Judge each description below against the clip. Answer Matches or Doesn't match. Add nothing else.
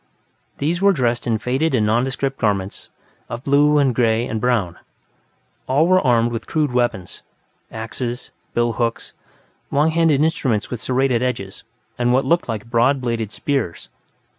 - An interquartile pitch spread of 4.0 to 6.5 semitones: Doesn't match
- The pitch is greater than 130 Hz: Doesn't match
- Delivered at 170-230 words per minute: Doesn't match